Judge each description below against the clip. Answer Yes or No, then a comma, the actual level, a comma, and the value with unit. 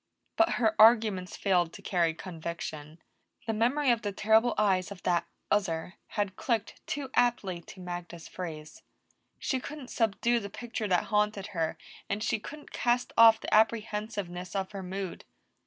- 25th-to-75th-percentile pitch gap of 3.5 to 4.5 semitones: Yes, average, 4.0 semitones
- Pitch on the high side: Yes, high, 205 Hz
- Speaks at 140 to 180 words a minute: Yes, average, 155 wpm